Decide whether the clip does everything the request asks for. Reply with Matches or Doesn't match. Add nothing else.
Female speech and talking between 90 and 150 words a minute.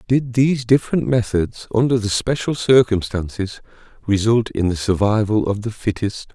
Doesn't match